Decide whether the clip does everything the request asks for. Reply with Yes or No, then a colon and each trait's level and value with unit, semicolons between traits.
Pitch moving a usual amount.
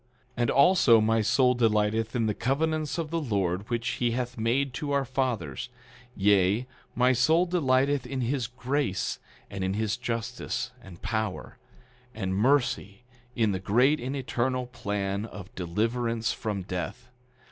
Yes: average, 3.8 semitones